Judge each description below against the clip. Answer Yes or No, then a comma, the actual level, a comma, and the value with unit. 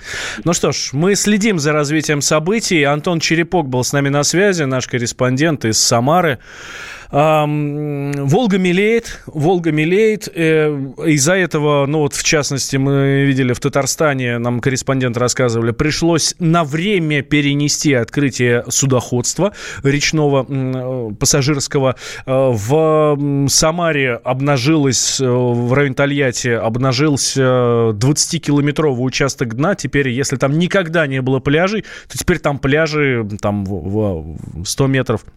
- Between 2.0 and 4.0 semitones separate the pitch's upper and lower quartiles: Yes, average, 3.4 semitones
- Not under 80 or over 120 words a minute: Yes, average, 115 wpm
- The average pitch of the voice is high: No, medium, 140 Hz